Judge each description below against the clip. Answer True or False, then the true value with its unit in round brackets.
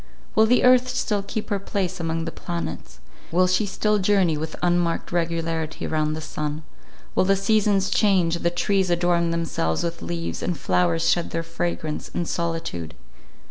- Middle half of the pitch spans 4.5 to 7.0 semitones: False (3.1 semitones)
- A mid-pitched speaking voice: True (170 Hz)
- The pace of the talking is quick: False (165 wpm)